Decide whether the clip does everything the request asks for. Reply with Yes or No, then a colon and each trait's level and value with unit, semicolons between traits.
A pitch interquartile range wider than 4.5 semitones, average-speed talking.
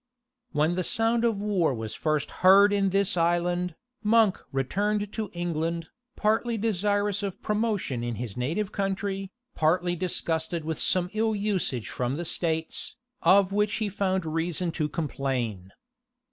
No: average, 4.2 semitones; average, 145 wpm